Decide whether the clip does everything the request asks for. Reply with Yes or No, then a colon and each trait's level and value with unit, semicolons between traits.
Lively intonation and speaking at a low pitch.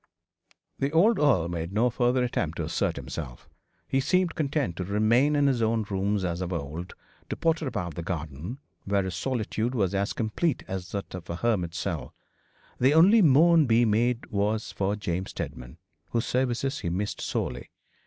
Yes: wide, 6.7 semitones; low, 110 Hz